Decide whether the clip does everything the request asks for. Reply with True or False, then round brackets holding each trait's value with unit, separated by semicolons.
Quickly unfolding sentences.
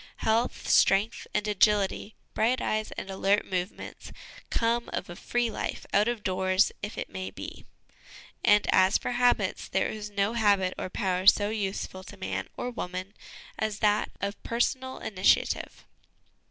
False (155 wpm)